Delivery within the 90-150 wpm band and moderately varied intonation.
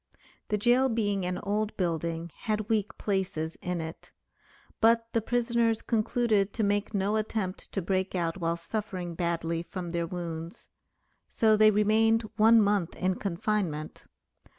Yes: average, 145 wpm; average, 4.1 semitones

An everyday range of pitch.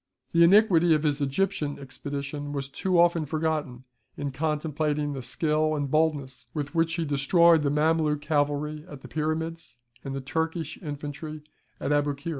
No: narrow, 2.1 semitones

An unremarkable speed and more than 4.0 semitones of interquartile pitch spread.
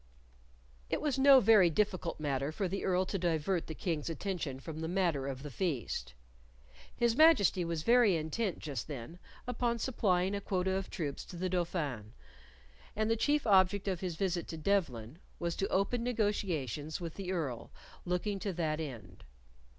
Yes: average, 170 wpm; average, 4.5 semitones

